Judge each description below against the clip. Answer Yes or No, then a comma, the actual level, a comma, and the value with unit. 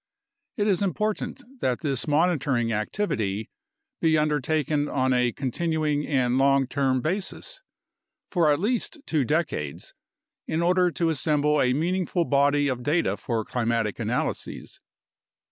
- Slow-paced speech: Yes, slow, 130 wpm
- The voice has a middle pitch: Yes, medium, 150 Hz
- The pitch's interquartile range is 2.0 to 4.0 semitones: No, average, 4.9 semitones